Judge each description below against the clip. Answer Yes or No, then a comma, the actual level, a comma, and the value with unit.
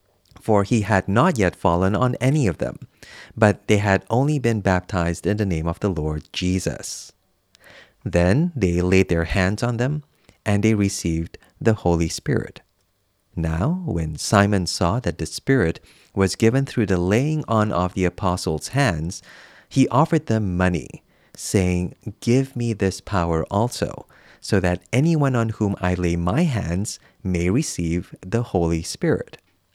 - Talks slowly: No, average, 155 wpm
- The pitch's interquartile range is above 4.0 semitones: Yes, average, 4.5 semitones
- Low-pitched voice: Yes, low, 100 Hz